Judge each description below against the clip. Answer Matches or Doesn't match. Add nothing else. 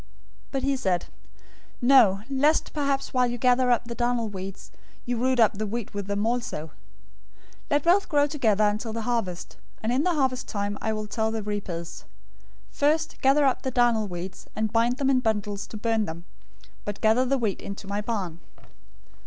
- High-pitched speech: Matches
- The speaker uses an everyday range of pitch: Matches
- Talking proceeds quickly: Doesn't match